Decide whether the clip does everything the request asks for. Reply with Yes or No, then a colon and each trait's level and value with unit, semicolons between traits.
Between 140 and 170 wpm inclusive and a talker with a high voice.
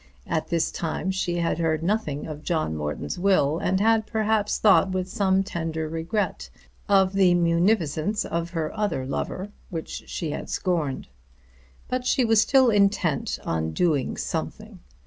No: average, 150 wpm; medium, 180 Hz